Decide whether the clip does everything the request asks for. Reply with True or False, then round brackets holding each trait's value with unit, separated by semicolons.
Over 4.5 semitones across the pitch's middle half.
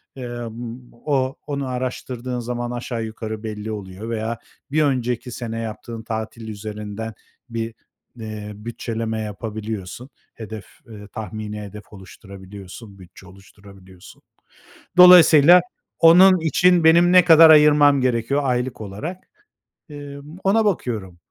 True (4.9 semitones)